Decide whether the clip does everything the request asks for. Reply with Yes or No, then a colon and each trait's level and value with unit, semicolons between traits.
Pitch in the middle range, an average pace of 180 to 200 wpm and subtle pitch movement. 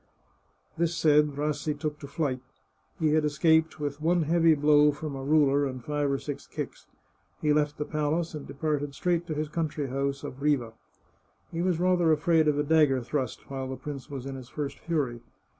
Yes: medium, 150 Hz; average, 190 wpm; narrow, 2.1 semitones